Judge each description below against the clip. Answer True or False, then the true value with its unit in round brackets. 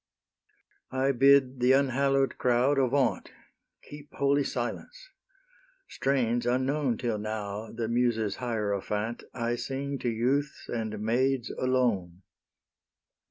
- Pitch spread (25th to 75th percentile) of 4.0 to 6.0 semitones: False (3.4 semitones)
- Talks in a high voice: False (125 Hz)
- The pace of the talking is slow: True (105 wpm)